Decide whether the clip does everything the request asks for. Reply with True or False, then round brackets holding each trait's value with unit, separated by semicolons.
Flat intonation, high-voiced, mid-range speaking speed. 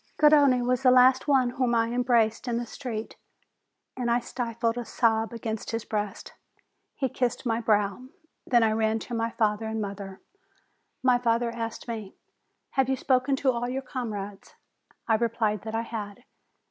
True (2.2 semitones; 235 Hz; 170 wpm)